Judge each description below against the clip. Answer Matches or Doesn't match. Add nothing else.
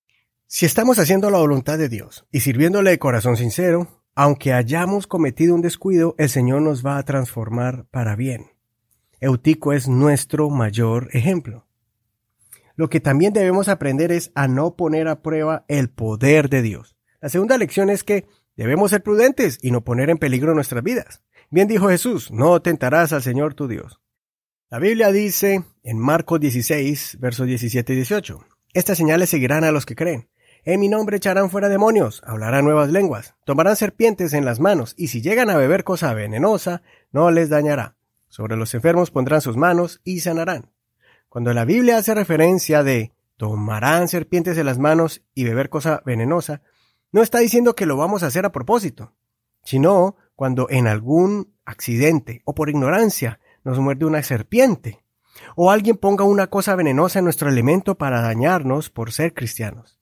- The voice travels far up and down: Matches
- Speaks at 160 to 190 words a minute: Matches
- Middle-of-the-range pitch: Matches